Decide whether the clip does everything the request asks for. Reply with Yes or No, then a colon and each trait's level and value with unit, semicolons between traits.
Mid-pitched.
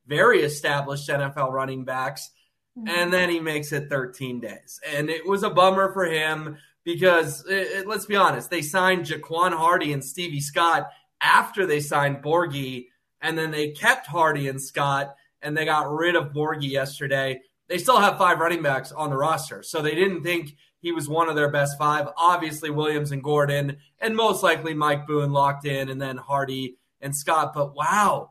Yes: medium, 150 Hz